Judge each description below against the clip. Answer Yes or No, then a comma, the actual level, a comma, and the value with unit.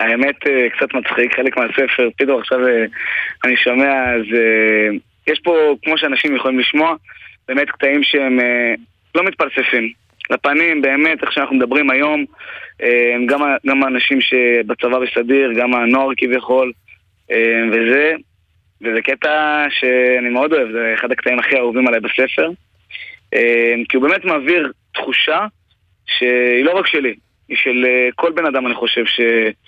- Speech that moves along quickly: No, average, 130 wpm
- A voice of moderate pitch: No, low, 125 Hz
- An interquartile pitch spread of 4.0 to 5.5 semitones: No, average, 2.8 semitones